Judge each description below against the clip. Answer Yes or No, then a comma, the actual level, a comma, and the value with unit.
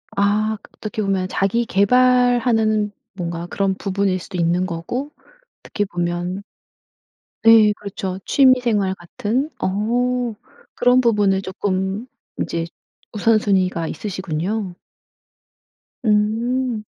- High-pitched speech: Yes, high, 205 Hz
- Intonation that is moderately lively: Yes, average, 3.4 semitones